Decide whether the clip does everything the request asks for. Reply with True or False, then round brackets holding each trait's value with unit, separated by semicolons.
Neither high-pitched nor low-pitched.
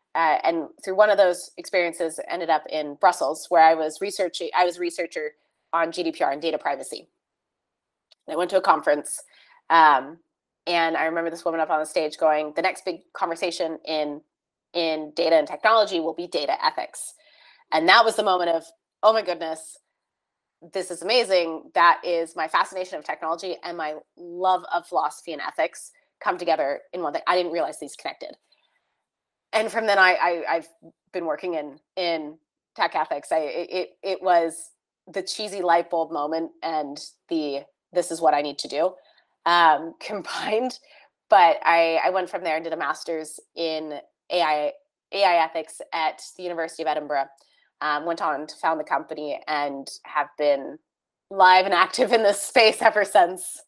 True (170 Hz)